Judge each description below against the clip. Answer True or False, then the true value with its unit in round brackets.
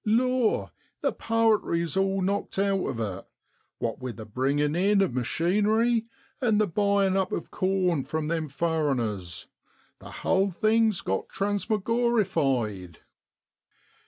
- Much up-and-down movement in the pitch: True (7.3 semitones)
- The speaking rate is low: True (130 wpm)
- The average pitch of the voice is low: False (190 Hz)